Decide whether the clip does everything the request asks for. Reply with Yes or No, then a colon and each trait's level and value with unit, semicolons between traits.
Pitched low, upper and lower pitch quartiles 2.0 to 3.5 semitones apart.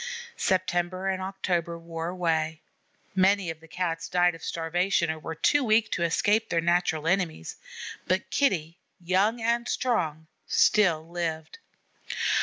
No: medium, 175 Hz; average, 2.8 semitones